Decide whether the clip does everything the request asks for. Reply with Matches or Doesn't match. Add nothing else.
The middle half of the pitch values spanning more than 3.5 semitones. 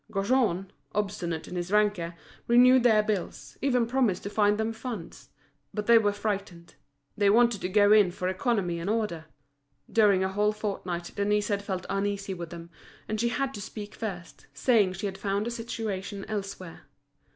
Doesn't match